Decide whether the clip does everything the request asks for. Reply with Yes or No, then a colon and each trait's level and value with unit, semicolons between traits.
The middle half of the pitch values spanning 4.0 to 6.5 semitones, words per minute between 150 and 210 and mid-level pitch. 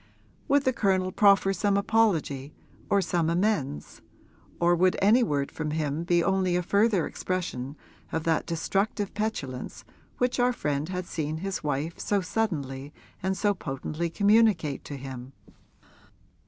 No: average, 5.2 semitones; average, 140 wpm; medium, 175 Hz